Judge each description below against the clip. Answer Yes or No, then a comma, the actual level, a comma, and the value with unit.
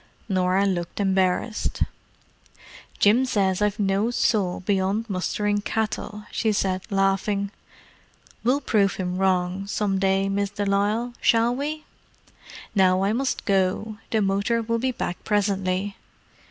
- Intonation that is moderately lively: No, narrow, 2.2 semitones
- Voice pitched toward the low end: No, high, 200 Hz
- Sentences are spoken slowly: Yes, slow, 125 wpm